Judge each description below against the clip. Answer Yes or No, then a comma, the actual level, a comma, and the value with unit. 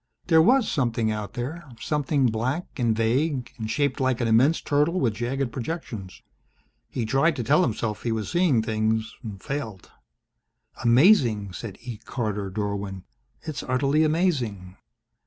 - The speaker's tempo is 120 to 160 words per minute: Yes, average, 140 wpm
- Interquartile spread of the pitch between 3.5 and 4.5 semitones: No, average, 5.0 semitones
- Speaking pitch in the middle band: No, low, 120 Hz